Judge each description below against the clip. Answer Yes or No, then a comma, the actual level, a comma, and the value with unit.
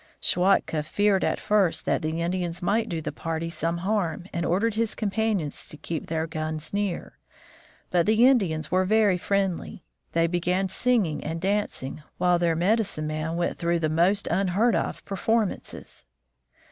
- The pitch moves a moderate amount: Yes, average, 3.7 semitones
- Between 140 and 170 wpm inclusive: Yes, average, 160 wpm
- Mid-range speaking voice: Yes, medium, 180 Hz